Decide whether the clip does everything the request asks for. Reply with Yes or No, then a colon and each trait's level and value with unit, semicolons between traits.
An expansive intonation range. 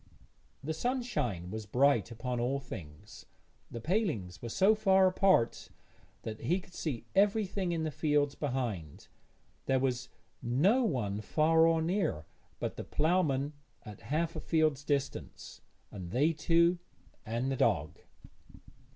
Yes: wide, 6.6 semitones